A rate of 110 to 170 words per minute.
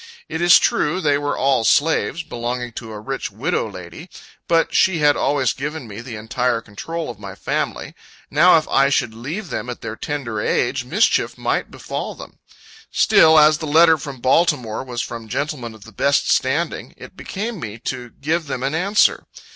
No: average, 185 wpm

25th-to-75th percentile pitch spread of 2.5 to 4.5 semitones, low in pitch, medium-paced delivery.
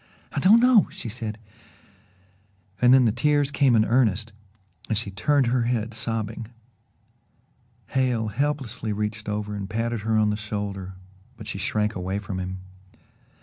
Yes: average, 3.0 semitones; low, 110 Hz; average, 155 wpm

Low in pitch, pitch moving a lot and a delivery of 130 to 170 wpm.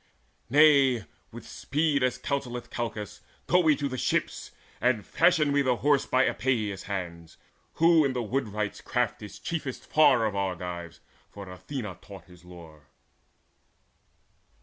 Yes: low, 120 Hz; wide, 6.2 semitones; average, 140 wpm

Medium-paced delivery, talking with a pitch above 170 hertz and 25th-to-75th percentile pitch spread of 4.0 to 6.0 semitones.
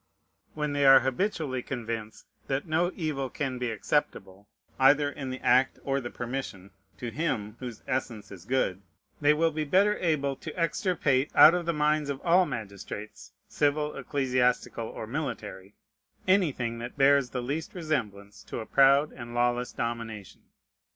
No: average, 155 wpm; low, 135 Hz; average, 4.3 semitones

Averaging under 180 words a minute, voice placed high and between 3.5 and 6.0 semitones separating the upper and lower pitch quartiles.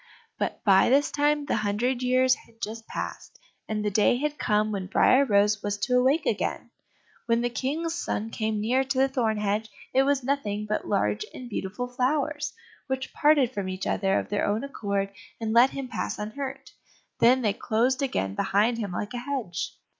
No: average, 190 wpm; high, 235 Hz; average, 4.3 semitones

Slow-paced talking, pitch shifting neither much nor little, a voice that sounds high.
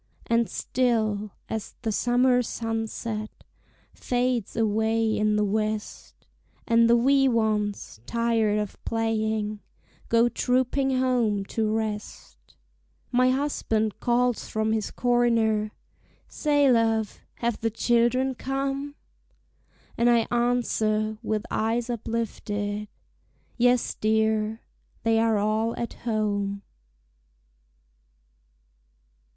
No: slow, 100 wpm; narrow, 2.1 semitones; high, 225 Hz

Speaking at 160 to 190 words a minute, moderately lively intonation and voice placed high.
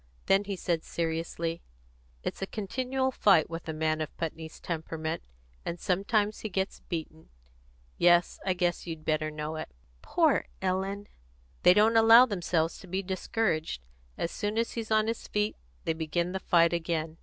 No: average, 165 wpm; average, 4.1 semitones; medium, 175 Hz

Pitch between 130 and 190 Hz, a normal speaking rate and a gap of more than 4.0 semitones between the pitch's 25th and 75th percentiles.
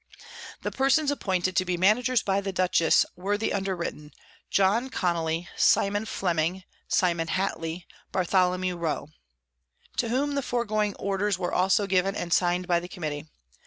No: medium, 185 Hz; average, 150 wpm; average, 2.7 semitones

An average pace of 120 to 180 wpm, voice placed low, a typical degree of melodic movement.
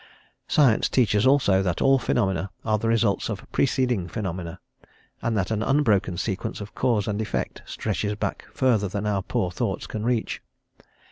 Yes: average, 160 wpm; low, 105 Hz; average, 3.4 semitones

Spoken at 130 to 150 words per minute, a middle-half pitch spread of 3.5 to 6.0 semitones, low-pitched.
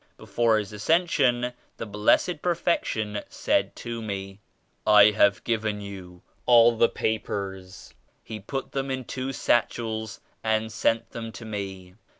No: average, 140 wpm; average, 2.7 semitones; low, 110 Hz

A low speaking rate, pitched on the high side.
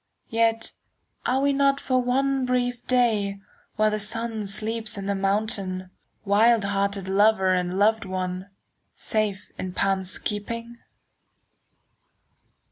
Yes: slow, 125 wpm; high, 215 Hz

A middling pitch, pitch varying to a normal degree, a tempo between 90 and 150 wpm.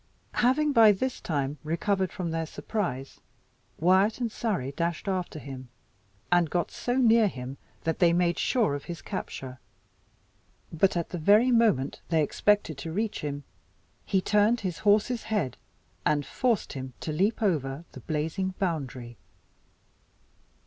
No: medium, 175 Hz; wide, 6.0 semitones; average, 145 wpm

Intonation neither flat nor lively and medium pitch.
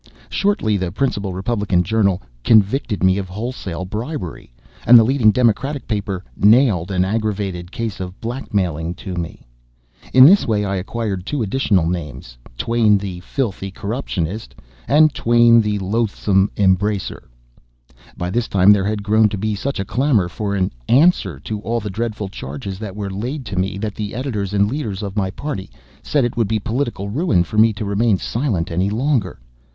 No: average, 3.7 semitones; low, 105 Hz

